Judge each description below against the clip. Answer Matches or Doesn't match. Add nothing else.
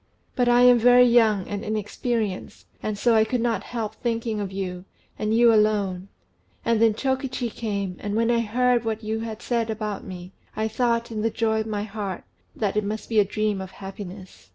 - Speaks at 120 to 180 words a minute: Doesn't match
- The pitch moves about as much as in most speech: Doesn't match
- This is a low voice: Doesn't match